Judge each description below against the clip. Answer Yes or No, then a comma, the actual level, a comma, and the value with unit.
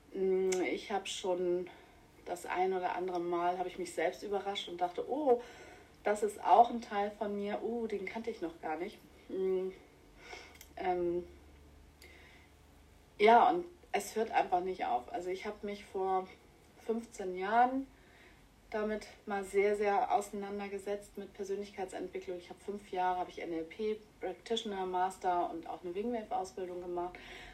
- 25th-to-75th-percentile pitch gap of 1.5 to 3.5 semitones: No, average, 4.5 semitones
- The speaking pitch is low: No, high, 200 Hz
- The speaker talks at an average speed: Yes, average, 150 wpm